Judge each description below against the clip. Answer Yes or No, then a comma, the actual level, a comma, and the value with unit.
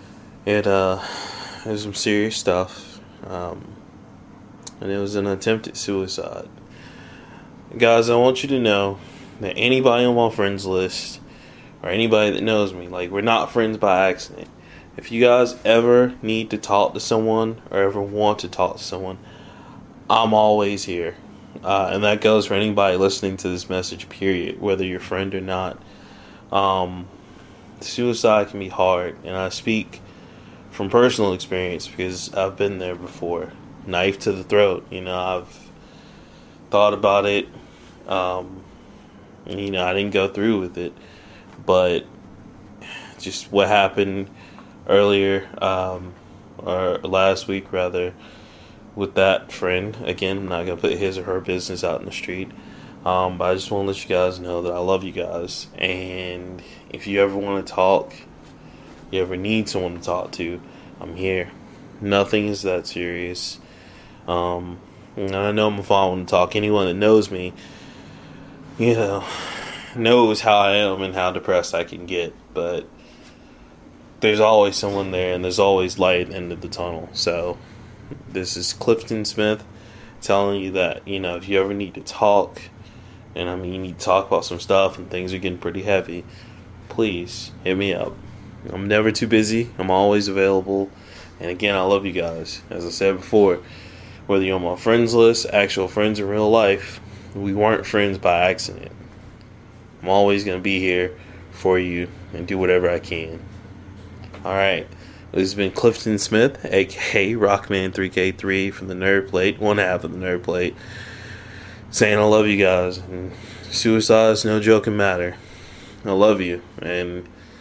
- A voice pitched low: Yes, low, 100 Hz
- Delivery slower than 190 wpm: Yes, average, 165 wpm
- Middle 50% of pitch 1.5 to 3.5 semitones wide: Yes, narrow, 2.5 semitones